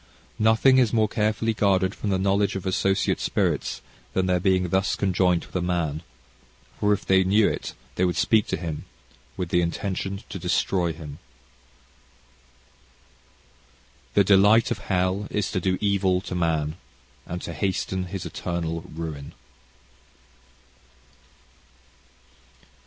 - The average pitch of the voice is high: No, very low, 95 Hz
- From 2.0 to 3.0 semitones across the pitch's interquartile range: Yes, narrow, 2.4 semitones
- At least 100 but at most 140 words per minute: Yes, slow, 135 wpm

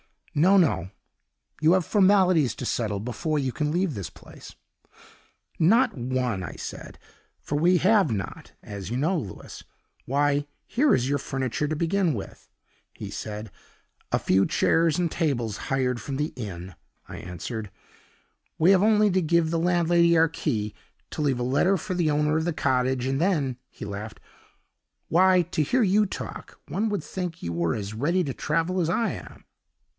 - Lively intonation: Yes, wide, 6.5 semitones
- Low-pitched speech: No, medium, 150 Hz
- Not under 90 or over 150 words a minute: No, average, 175 wpm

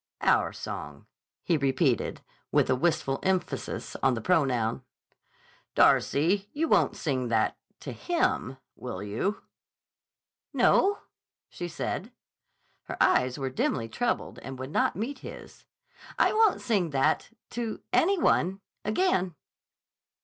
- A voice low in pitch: No, medium, 160 Hz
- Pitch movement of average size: No, wide, 8.6 semitones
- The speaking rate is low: Yes, slow, 110 wpm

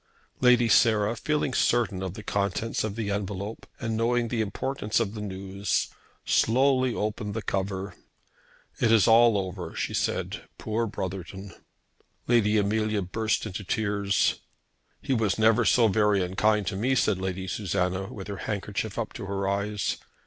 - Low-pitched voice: Yes, low, 105 Hz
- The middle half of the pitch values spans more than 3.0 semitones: No, narrow, 2.5 semitones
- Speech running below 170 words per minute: Yes, average, 155 wpm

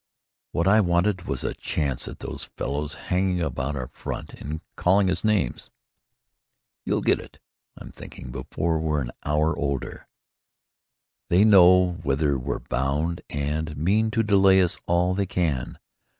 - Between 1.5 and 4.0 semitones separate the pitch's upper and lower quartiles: No, average, 4.4 semitones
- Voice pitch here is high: No, very low, 85 Hz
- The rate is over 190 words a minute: No, average, 150 wpm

